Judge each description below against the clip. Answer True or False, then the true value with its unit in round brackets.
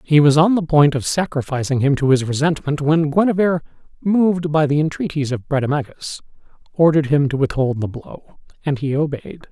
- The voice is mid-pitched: True (150 Hz)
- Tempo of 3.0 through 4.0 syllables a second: False (5.6 syllables/s)